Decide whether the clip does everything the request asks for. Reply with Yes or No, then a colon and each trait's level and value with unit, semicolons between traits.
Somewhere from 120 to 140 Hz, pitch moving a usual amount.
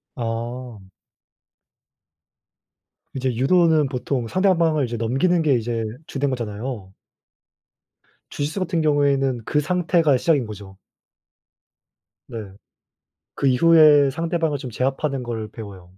Yes: low, 135 Hz; average, 5.0 semitones